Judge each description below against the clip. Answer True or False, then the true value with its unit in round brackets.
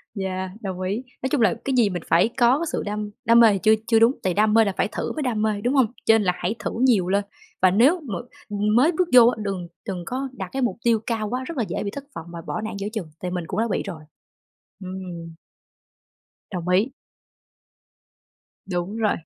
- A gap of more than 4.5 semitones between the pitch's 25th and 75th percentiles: False (4.2 semitones)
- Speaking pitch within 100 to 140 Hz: False (210 Hz)